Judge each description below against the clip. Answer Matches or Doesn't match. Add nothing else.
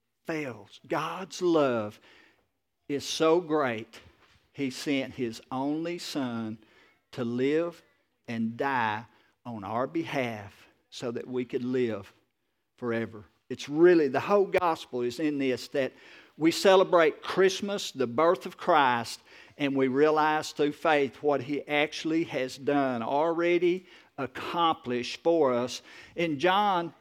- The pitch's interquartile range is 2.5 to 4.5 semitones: Doesn't match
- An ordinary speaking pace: Doesn't match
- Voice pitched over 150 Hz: Doesn't match